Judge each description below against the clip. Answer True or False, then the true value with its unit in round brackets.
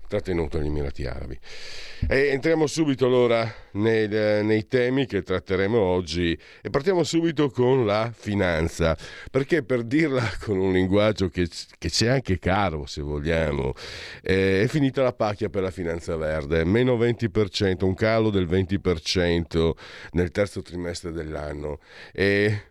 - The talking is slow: False (140 wpm)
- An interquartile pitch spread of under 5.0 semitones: False (5.5 semitones)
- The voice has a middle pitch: False (95 Hz)